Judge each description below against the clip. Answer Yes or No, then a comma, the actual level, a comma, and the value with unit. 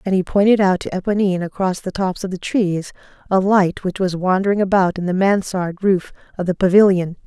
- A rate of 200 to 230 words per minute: Yes, fast, 205 wpm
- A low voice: No, high, 190 Hz